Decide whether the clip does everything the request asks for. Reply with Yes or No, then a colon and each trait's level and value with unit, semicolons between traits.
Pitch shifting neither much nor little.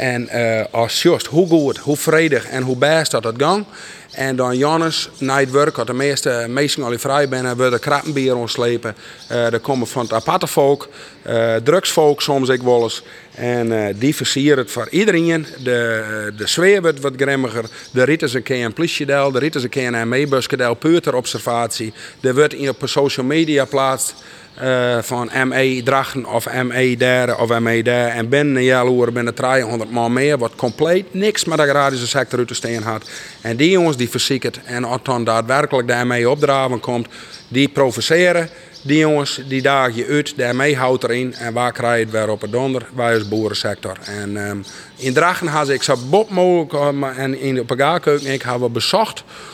Yes: average, 3.2 semitones